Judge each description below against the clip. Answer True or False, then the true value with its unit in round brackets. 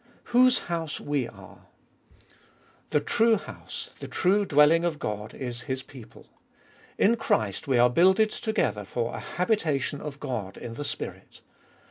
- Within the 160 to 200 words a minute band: False (145 wpm)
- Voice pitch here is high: False (145 Hz)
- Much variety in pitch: True (7.6 semitones)